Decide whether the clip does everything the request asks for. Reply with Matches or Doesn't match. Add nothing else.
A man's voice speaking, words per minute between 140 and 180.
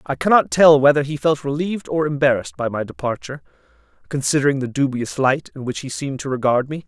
Doesn't match